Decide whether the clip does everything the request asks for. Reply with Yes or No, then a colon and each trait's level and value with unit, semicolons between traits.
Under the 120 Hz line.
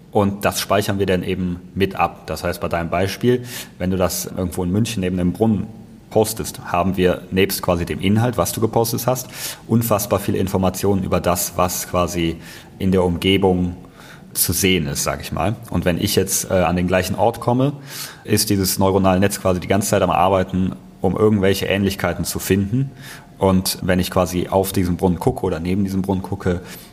Yes: very low, 95 Hz